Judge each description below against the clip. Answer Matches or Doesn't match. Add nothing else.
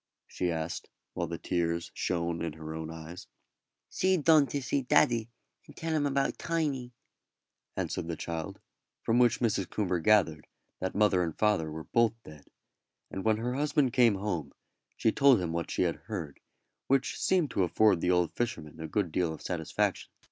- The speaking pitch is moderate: Doesn't match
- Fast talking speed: Doesn't match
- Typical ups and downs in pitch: Doesn't match